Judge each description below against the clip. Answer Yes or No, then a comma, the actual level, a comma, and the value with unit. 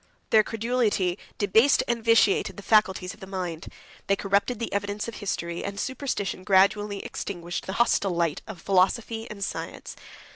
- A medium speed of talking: Yes, average, 155 wpm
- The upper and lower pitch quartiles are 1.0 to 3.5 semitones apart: Yes, average, 2.9 semitones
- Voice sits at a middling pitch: No, high, 200 Hz